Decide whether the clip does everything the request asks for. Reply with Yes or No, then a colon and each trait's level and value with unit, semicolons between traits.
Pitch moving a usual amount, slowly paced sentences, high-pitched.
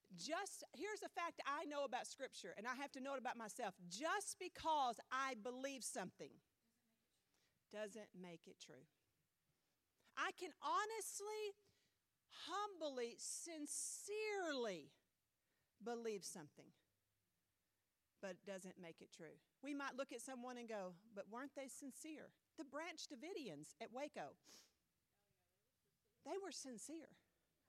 No: wide, 8.6 semitones; slow, 125 wpm; very high, 265 Hz